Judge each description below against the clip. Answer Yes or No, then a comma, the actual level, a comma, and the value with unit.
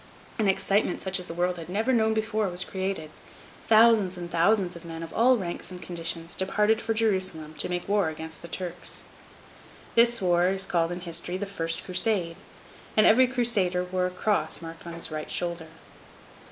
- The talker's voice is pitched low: No, medium, 185 Hz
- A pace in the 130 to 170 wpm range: No, average, 185 wpm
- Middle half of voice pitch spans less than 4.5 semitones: Yes, average, 3.8 semitones